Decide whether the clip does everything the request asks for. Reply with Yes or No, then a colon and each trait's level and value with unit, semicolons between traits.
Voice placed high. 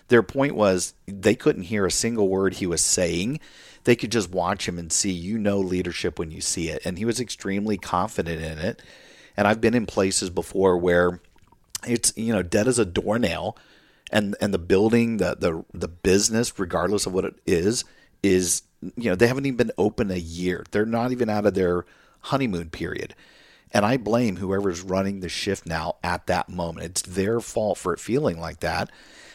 No: very low, 95 Hz